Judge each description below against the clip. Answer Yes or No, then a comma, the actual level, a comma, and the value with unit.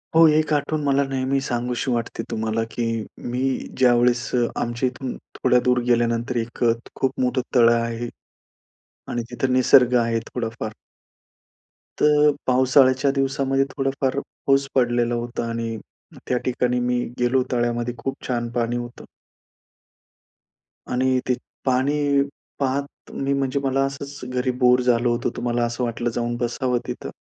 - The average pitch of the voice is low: Yes, low, 125 Hz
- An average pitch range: No, narrow, 2.0 semitones